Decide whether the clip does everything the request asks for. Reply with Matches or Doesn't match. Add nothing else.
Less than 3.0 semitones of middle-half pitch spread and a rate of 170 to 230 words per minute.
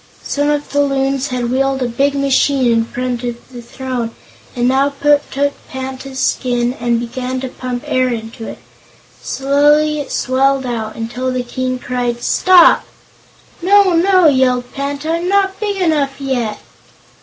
Doesn't match